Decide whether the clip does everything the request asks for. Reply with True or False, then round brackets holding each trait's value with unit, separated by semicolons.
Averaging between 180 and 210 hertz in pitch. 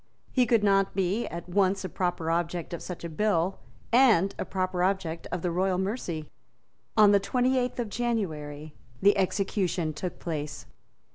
True (185 Hz)